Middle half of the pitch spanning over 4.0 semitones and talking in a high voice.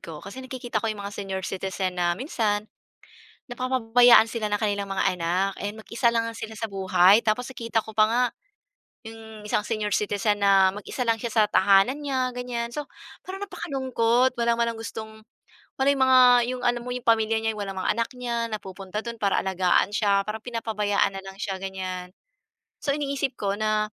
No: average, 3.3 semitones; high, 220 Hz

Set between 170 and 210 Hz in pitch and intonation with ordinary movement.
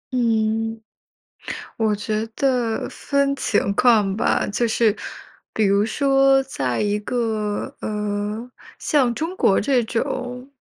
No: high, 225 Hz; average, 3.3 semitones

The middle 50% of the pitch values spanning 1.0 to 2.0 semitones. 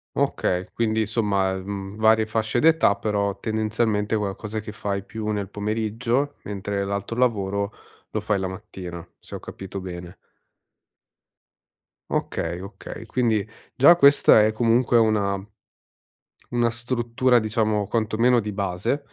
No: narrow, 2.6 semitones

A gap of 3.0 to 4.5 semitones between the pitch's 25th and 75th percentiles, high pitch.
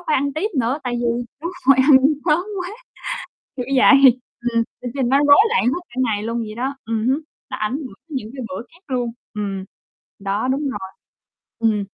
Yes: average, 3.8 semitones; high, 245 Hz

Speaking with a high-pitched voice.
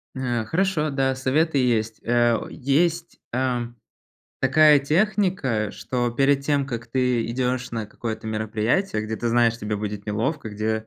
No: low, 125 Hz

